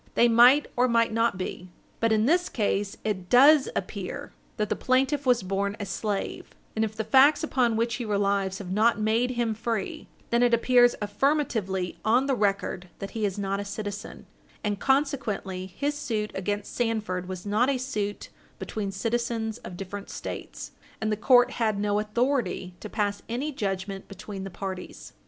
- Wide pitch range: No, average, 3.5 semitones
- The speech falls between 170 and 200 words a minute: Yes, average, 175 wpm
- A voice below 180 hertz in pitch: No, high, 215 Hz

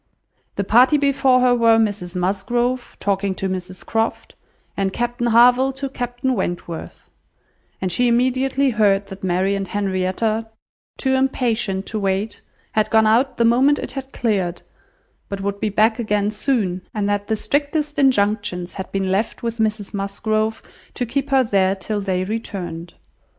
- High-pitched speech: Yes, high, 215 Hz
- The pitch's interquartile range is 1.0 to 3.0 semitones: No, average, 4.0 semitones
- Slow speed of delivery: No, average, 155 wpm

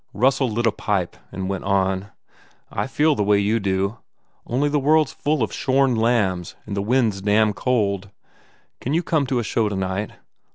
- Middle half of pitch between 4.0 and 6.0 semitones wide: Yes, average, 5.0 semitones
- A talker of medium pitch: No, low, 110 Hz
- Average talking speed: Yes, average, 195 wpm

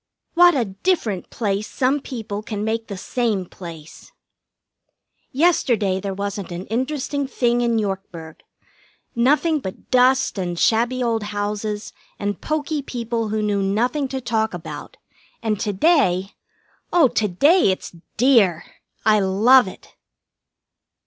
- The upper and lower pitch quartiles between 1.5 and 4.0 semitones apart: No, average, 4.6 semitones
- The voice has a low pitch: No, high, 220 Hz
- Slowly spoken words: Yes, slow, 130 wpm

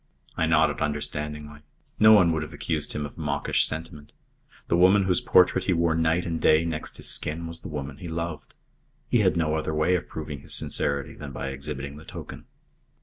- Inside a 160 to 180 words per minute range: No, average, 200 wpm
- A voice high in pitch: No, very low, 80 Hz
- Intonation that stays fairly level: Yes, narrow, 2.1 semitones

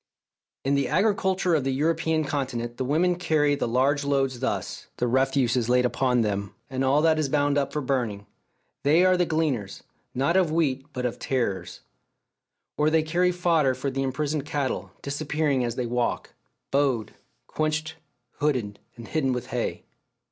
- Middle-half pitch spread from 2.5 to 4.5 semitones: Yes, average, 3.7 semitones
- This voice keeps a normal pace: Yes, average, 170 wpm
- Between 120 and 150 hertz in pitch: Yes, medium, 140 Hz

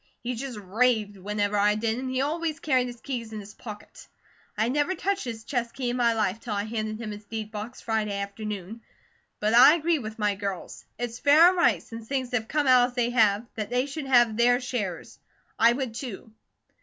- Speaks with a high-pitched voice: Yes, high, 230 Hz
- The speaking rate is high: Yes, fast, 215 wpm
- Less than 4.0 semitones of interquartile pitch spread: Yes, average, 3.2 semitones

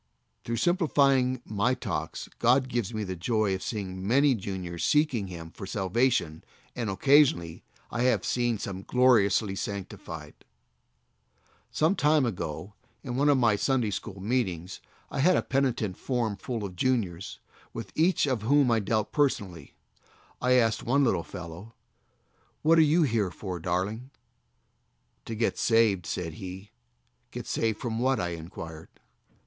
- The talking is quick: No, average, 150 wpm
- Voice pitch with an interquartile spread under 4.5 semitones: No, average, 5.3 semitones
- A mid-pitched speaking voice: No, low, 110 Hz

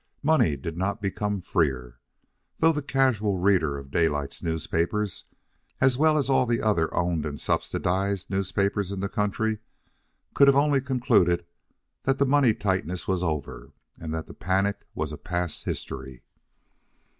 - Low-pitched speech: Yes, very low, 95 Hz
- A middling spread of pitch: No, wide, 6.1 semitones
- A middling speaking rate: Yes, average, 150 wpm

